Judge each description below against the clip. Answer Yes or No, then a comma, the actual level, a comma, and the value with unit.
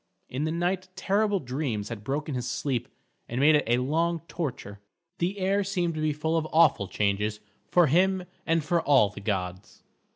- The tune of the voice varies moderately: No, wide, 6.4 semitones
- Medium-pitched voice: Yes, medium, 150 Hz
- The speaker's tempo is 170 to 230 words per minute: Yes, average, 185 wpm